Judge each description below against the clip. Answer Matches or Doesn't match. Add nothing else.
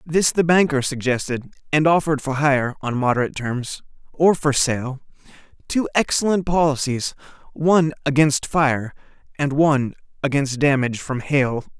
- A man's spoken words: Matches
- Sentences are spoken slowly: Matches